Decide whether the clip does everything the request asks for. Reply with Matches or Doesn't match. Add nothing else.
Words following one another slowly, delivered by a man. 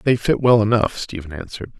Doesn't match